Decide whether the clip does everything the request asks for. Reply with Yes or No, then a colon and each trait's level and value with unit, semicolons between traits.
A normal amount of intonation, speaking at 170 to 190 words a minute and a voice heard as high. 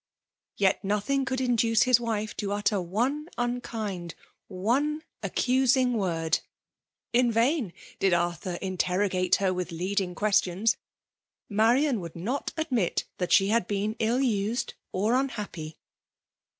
No: average, 4.8 semitones; slow, 135 wpm; high, 210 Hz